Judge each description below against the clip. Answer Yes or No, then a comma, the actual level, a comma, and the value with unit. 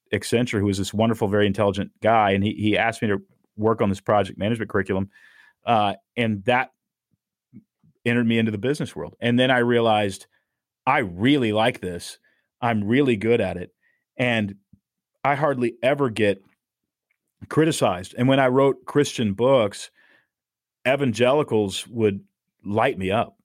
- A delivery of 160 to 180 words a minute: No, average, 150 wpm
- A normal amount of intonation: Yes, average, 3.4 semitones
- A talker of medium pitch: No, low, 110 Hz